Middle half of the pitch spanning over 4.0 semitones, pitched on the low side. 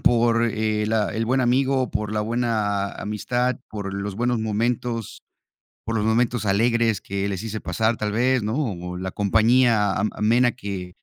No: average, 2.7 semitones; low, 110 Hz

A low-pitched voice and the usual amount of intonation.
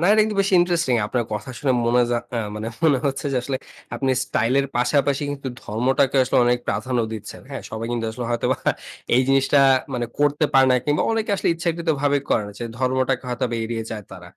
Yes: low, 130 Hz; average, 3.3 semitones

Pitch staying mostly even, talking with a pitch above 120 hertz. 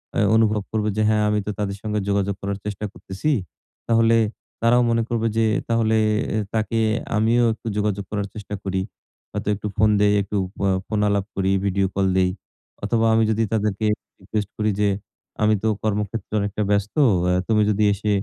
No: narrow, 1.6 semitones; low, 105 Hz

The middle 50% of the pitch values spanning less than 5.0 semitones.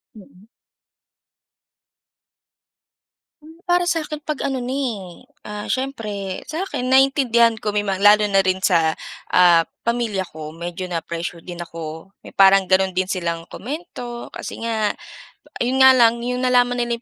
No: wide, 5.4 semitones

